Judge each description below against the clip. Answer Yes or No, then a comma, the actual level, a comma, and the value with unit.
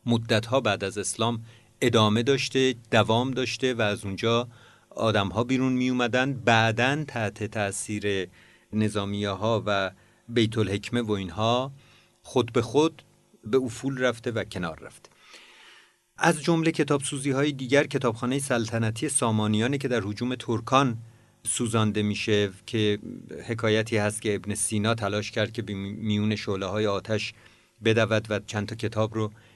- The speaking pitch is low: Yes, low, 115 Hz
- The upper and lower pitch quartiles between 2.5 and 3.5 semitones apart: Yes, average, 3.1 semitones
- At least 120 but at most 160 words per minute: Yes, average, 140 wpm